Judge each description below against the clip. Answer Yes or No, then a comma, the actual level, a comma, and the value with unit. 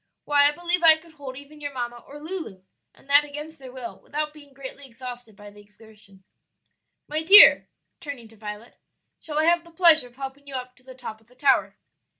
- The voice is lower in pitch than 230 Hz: No, very high, 275 Hz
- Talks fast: Yes, fast, 210 wpm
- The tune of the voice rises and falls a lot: No, average, 4.1 semitones